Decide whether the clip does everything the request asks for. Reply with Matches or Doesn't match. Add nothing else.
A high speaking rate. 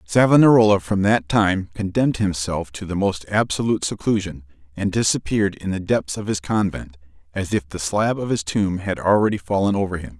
Doesn't match